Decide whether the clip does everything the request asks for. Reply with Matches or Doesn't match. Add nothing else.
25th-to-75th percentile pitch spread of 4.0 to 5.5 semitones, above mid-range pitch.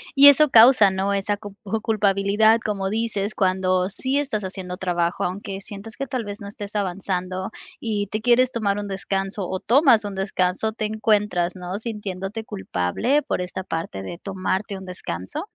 Doesn't match